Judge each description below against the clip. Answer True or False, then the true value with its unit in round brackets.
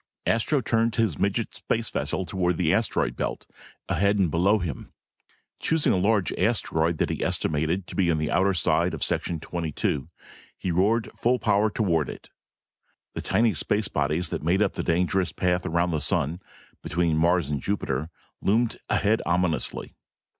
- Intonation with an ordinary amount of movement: True (4.1 semitones)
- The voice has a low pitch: True (90 Hz)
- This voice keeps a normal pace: True (170 wpm)